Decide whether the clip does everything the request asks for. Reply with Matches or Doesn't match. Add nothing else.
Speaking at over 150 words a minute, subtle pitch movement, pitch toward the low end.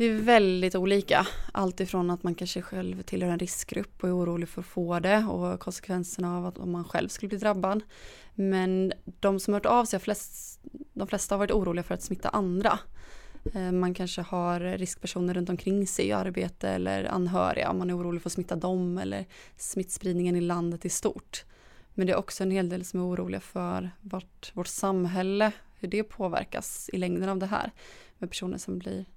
Doesn't match